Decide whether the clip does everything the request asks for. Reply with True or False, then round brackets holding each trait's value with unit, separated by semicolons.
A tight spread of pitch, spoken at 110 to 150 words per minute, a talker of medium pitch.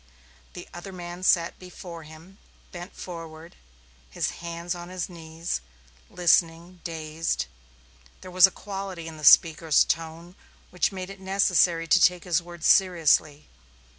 True (1.9 semitones; 135 wpm; 175 Hz)